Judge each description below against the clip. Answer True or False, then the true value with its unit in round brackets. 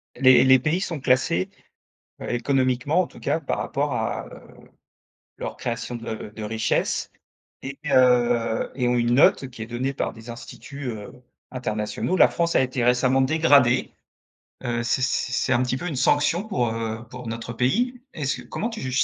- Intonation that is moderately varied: True (3.0 semitones)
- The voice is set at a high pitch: False (125 Hz)